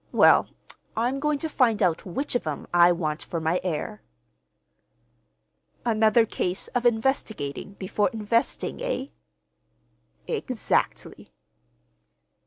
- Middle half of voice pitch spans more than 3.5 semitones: Yes, wide, 5.5 semitones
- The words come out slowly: Yes, slow, 105 wpm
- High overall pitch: Yes, high, 215 Hz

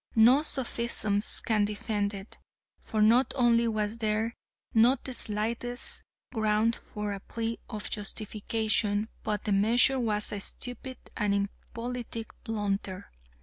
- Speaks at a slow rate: Yes, slow, 125 wpm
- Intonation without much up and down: Yes, narrow, 2.1 semitones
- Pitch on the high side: Yes, high, 220 Hz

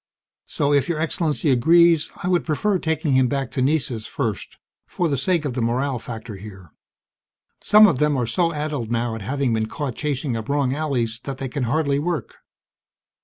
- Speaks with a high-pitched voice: No, medium, 140 Hz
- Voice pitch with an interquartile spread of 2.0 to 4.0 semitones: No, average, 4.5 semitones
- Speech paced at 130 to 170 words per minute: No, average, 195 wpm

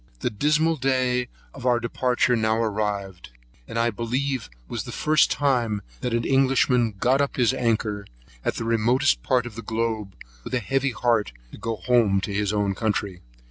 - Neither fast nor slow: Yes, average, 180 wpm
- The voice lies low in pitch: Yes, low, 115 Hz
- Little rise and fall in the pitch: No, average, 3.2 semitones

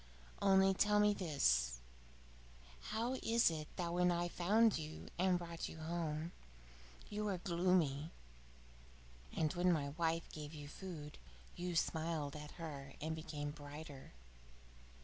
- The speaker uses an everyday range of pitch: Yes, average, 3.3 semitones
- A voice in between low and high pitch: Yes, medium, 165 Hz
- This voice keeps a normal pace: No, slow, 130 wpm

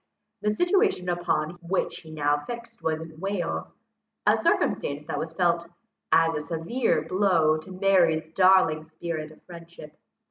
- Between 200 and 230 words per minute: No, average, 145 wpm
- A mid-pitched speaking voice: Yes, medium, 170 Hz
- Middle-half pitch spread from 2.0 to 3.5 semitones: Yes, average, 3.1 semitones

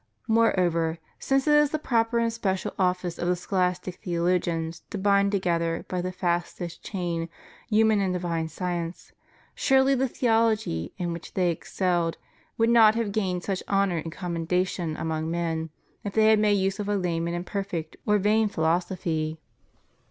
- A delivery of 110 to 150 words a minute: No, average, 165 wpm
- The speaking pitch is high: No, medium, 180 Hz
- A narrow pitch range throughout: No, average, 3.7 semitones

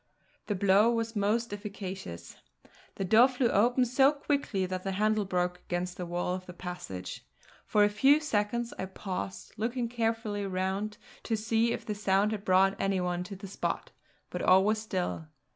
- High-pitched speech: Yes, high, 205 Hz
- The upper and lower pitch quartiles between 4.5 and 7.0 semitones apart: No, average, 3.4 semitones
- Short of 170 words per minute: No, average, 175 wpm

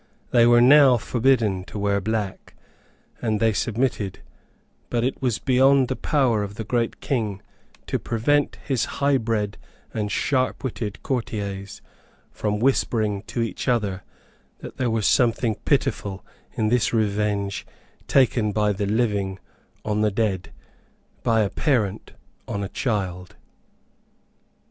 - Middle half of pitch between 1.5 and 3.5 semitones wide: Yes, average, 3.2 semitones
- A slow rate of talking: Yes, slow, 130 wpm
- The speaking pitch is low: Yes, low, 110 Hz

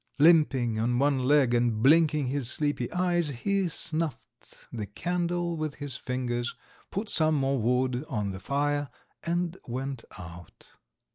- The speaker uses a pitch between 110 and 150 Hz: Yes, medium, 140 Hz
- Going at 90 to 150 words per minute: Yes, average, 140 wpm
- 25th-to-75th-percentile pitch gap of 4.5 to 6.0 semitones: Yes, average, 4.9 semitones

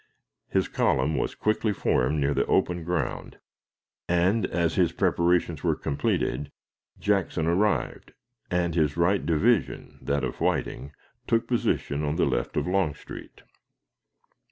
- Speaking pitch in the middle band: No, very low, 85 Hz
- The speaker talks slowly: Yes, slow, 130 wpm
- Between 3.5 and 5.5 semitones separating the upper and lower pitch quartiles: Yes, average, 4.3 semitones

